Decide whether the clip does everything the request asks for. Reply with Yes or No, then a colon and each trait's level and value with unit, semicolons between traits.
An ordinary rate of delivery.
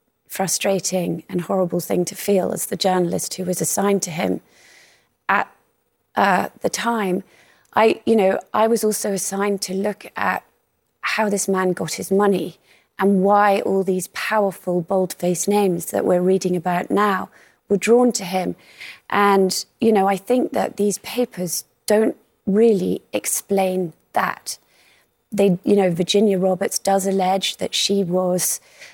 Yes: average, 150 wpm